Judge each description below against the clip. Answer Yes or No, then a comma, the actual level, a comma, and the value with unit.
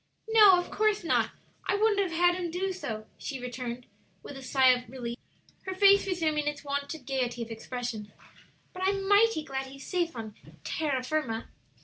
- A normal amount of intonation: No, wide, 6.8 semitones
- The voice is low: No, very high, 295 Hz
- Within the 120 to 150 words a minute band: No, average, 175 wpm